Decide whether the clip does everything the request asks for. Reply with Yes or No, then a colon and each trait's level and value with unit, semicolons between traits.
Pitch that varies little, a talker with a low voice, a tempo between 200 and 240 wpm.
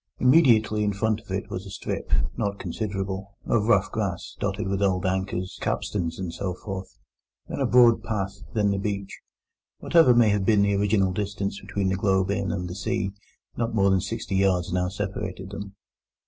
No: narrow, 1.8 semitones; low, 100 Hz; average, 170 wpm